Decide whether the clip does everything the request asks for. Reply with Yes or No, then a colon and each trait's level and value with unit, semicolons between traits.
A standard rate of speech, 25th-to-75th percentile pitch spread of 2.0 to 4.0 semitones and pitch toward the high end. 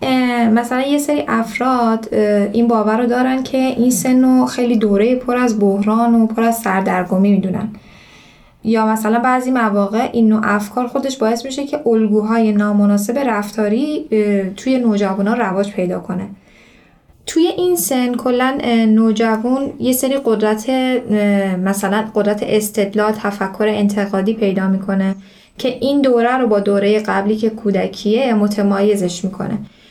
Yes: average, 135 wpm; average, 3.3 semitones; high, 220 Hz